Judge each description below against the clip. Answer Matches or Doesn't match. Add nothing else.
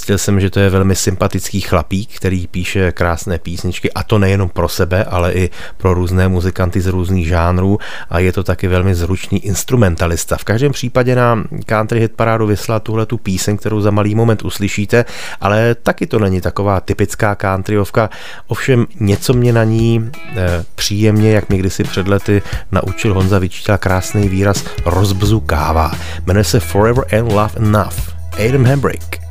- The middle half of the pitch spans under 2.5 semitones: Doesn't match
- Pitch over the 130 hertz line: Doesn't match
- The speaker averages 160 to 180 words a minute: Matches